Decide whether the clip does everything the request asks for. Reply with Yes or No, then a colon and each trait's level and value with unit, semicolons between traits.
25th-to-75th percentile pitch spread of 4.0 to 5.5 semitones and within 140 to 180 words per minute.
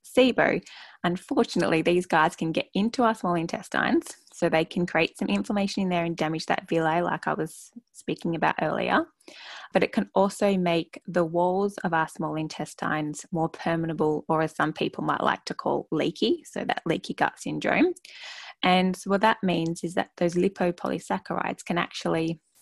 Yes: average, 4.7 semitones; average, 175 wpm